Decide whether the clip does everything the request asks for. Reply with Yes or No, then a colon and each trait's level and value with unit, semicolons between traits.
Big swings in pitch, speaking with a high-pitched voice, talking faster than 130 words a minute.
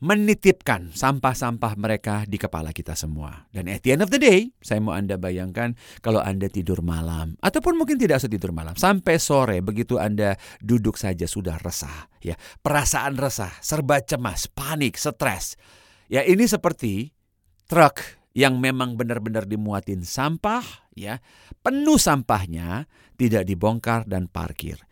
No: wide, 6.9 semitones; low, 110 Hz; fast, 140 wpm